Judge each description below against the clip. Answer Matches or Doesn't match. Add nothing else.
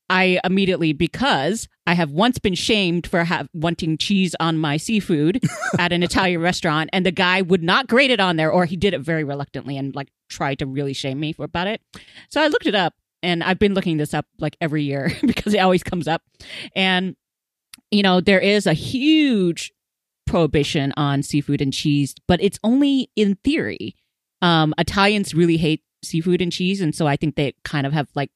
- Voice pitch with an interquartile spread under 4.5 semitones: Matches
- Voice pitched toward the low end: Doesn't match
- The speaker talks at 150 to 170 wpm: Doesn't match